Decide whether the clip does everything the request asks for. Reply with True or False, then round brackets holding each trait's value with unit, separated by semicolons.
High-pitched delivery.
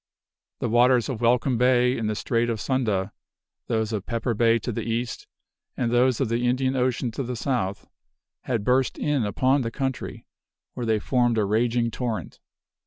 False (120 Hz)